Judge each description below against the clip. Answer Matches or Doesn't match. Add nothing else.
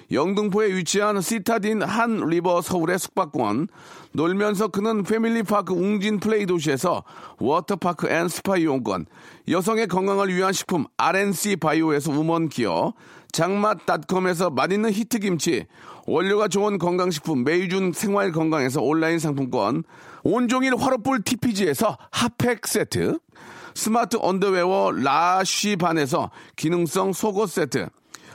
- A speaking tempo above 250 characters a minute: Matches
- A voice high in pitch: Matches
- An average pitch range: Matches